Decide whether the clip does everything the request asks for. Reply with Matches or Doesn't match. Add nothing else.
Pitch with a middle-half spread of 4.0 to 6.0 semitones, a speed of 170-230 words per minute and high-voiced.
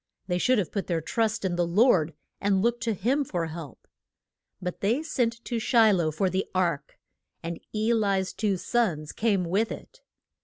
Matches